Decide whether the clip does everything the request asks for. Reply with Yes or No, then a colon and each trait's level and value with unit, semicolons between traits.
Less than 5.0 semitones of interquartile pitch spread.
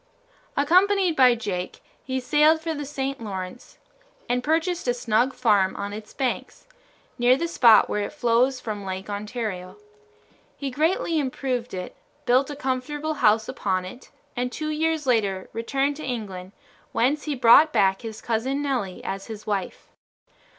No: wide, 5.6 semitones